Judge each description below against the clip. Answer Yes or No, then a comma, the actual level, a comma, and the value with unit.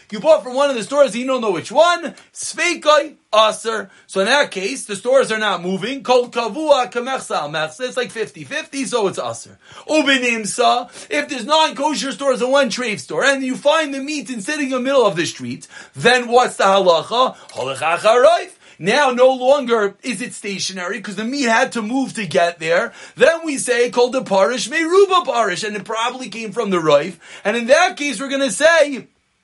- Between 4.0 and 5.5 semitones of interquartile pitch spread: Yes, average, 4.8 semitones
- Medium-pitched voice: No, very high, 250 Hz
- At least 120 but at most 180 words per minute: No, average, 200 wpm